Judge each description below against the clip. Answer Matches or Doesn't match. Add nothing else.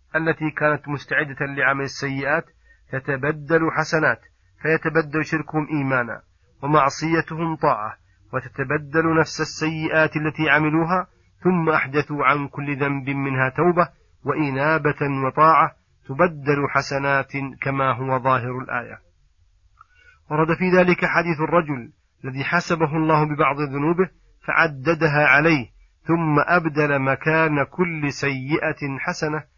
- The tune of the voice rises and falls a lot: Doesn't match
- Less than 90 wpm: Doesn't match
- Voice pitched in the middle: Matches